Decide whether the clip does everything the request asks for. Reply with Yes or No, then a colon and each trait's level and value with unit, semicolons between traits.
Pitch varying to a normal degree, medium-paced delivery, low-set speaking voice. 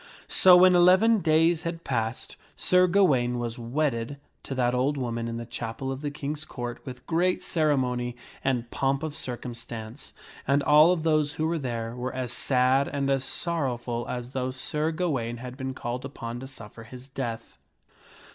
Yes: average, 4.1 semitones; average, 175 wpm; low, 130 Hz